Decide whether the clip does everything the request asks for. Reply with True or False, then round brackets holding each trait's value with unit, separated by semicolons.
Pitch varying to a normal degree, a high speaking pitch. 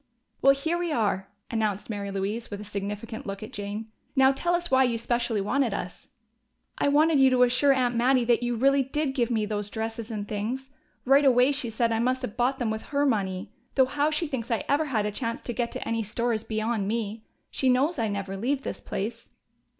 True (3.7 semitones; 235 Hz)